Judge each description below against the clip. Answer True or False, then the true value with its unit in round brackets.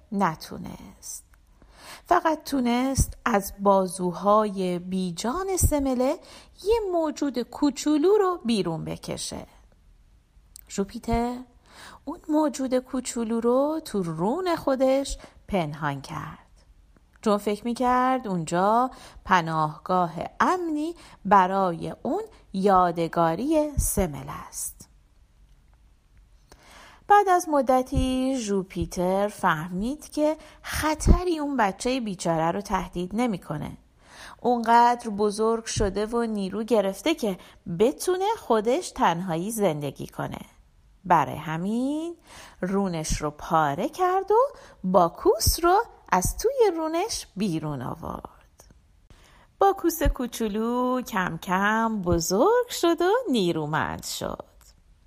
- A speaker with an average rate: False (90 wpm)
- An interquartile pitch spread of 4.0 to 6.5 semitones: False (8.5 semitones)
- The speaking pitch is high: True (225 Hz)